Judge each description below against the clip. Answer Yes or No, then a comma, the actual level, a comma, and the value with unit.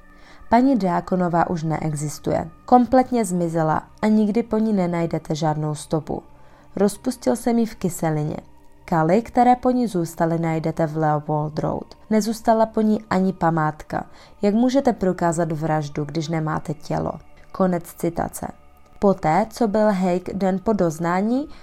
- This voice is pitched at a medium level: Yes, medium, 180 Hz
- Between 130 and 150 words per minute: Yes, average, 135 wpm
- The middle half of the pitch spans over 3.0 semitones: Yes, wide, 5.5 semitones